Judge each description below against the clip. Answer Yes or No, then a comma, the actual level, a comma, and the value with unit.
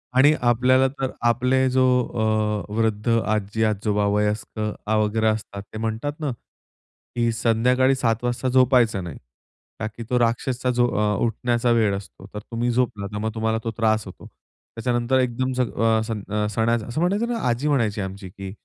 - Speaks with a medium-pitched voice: No, low, 115 Hz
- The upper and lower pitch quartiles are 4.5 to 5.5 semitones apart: No, average, 2.8 semitones